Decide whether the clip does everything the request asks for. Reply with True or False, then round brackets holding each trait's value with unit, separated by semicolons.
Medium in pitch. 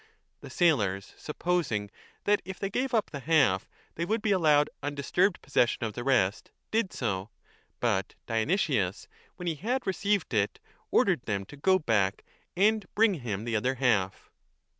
True (145 Hz)